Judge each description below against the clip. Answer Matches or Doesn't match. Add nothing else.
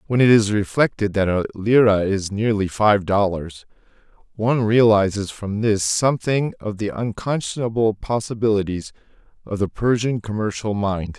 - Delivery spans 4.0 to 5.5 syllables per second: Matches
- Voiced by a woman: Doesn't match